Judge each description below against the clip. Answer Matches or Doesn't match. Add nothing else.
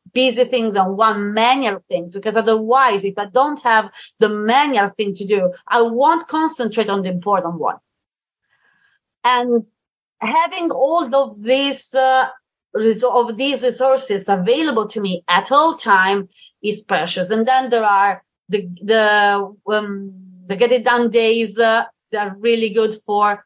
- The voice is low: Doesn't match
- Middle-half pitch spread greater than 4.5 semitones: Doesn't match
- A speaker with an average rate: Matches